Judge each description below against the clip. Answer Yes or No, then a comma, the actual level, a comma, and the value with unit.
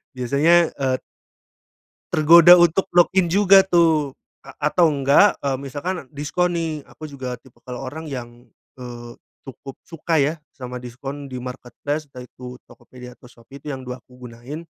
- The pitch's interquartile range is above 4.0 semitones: Yes, average, 4.4 semitones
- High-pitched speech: No, medium, 140 Hz